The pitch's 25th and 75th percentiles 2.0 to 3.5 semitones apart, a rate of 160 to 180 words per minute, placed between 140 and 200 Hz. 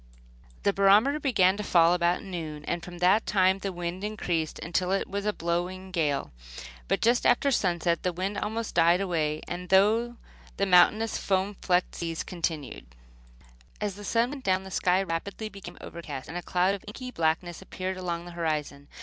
Yes: average, 2.9 semitones; average, 175 wpm; medium, 185 Hz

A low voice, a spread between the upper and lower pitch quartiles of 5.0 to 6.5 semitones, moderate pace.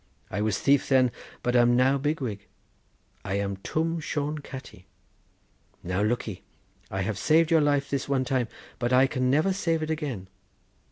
Yes: low, 130 Hz; average, 5.3 semitones; average, 170 wpm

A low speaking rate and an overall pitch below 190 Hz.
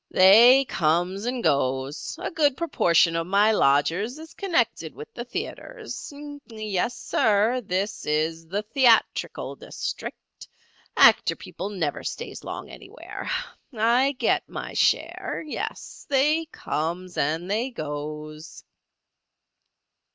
No: slow, 115 wpm; high, 200 Hz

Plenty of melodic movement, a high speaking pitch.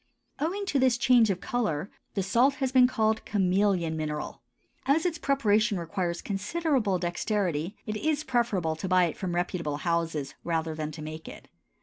Yes: wide, 6.5 semitones; high, 195 Hz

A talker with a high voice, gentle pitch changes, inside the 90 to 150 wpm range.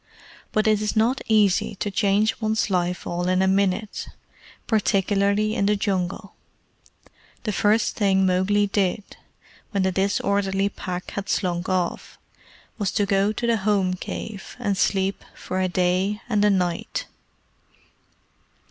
Yes: high, 200 Hz; narrow, 1.9 semitones; average, 140 wpm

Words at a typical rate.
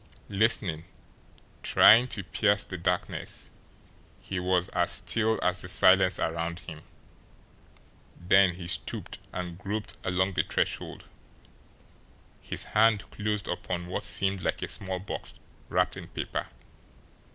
No: slow, 125 wpm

